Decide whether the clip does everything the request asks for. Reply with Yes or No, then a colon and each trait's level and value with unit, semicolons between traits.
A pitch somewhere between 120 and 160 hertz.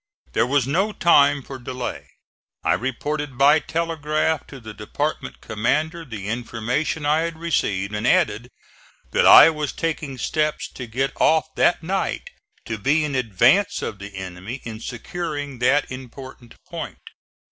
Yes: medium, 140 Hz